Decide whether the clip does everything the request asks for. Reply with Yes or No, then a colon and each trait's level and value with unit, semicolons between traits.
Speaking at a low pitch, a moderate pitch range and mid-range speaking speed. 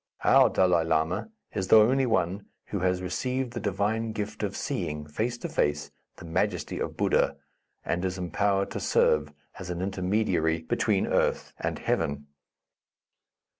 Yes: very low, 95 Hz; average, 4.3 semitones; average, 150 wpm